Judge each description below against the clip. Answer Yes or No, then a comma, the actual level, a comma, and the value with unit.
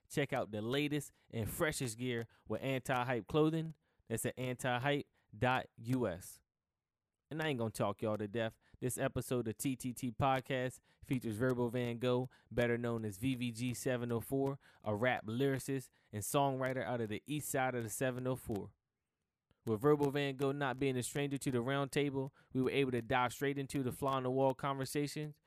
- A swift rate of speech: No, average, 165 wpm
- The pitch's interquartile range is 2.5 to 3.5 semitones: Yes, average, 2.9 semitones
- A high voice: No, low, 125 Hz